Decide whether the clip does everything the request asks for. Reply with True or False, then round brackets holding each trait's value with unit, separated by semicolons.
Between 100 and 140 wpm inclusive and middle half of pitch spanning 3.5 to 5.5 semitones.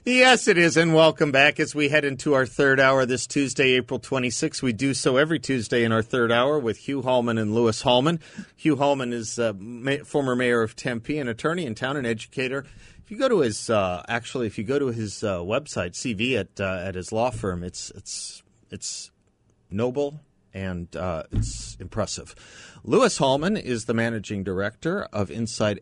False (200 wpm; 4.7 semitones)